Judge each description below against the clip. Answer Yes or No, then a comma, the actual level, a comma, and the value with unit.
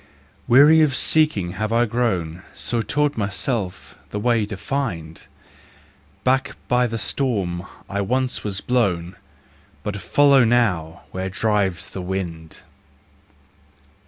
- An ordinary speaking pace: No, slow, 120 wpm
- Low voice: Yes, low, 105 Hz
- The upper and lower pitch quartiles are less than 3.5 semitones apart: No, average, 5.1 semitones